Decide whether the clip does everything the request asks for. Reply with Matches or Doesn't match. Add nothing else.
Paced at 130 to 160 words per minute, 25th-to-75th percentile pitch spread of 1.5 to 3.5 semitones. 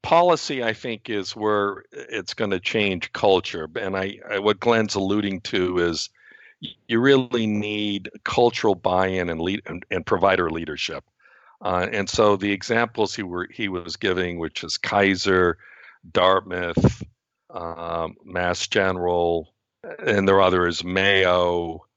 Matches